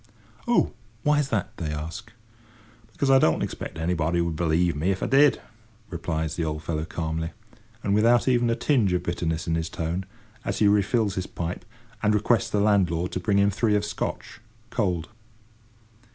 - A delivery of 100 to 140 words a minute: No, average, 175 wpm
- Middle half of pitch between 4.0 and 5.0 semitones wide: Yes, average, 4.6 semitones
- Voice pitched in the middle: No, very low, 90 Hz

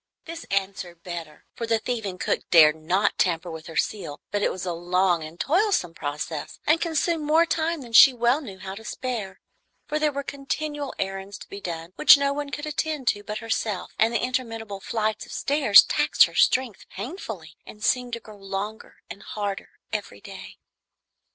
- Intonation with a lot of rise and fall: Yes, wide, 6.8 semitones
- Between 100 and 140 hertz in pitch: No, high, 215 Hz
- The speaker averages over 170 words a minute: Yes, average, 190 wpm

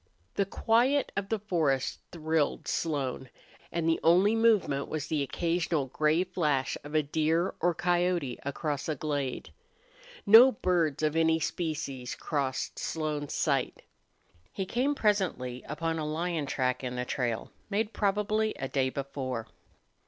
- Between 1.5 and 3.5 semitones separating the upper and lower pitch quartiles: No, average, 4.7 semitones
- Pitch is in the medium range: Yes, medium, 160 Hz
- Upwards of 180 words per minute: No, average, 140 wpm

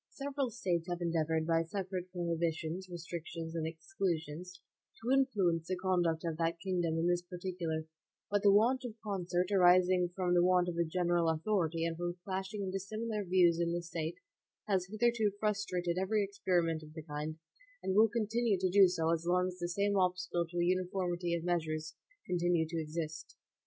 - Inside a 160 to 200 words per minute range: Yes, average, 180 wpm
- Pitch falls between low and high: Yes, medium, 175 Hz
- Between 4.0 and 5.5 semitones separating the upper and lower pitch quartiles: No, narrow, 2.5 semitones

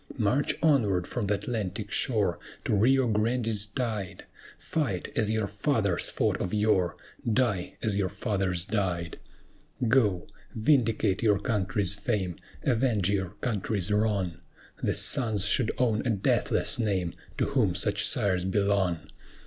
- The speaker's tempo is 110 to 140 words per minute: Yes, slow, 135 wpm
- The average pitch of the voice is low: Yes, low, 105 Hz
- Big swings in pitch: No, average, 3.0 semitones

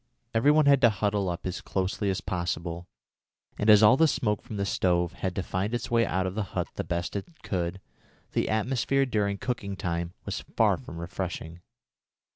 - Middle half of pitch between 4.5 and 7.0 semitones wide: No, average, 4.1 semitones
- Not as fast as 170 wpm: No, average, 200 wpm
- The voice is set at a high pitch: No, low, 100 Hz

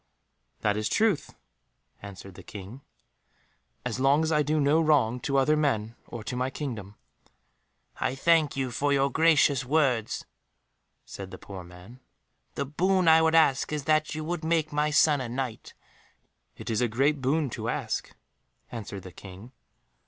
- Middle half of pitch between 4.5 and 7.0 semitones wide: Yes, average, 5.3 semitones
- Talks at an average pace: Yes, average, 165 wpm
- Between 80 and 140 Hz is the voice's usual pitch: Yes, low, 135 Hz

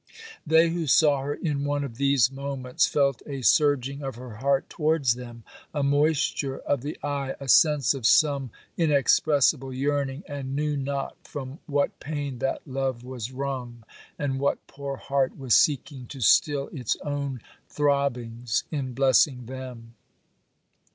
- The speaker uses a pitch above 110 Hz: Yes, medium, 140 Hz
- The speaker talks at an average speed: Yes, average, 150 wpm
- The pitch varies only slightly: Yes, narrow, 1.9 semitones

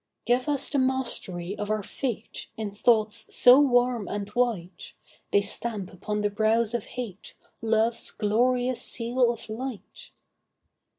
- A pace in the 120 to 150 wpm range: Yes, slow, 135 wpm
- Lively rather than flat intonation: No, average, 3.0 semitones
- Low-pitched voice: No, high, 230 Hz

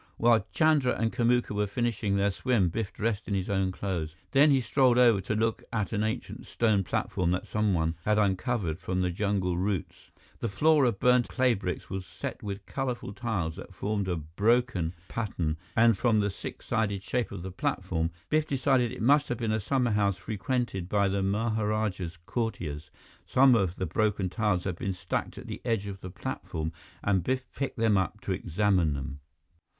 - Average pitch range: Yes, average, 4.1 semitones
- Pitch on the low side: Yes, low, 105 Hz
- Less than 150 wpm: No, average, 185 wpm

